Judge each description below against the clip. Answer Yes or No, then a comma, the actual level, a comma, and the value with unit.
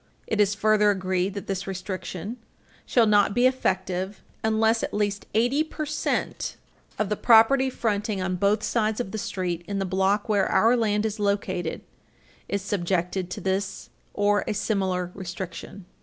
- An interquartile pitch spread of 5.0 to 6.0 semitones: No, narrow, 2.5 semitones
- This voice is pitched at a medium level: No, high, 200 Hz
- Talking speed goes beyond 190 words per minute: No, average, 160 wpm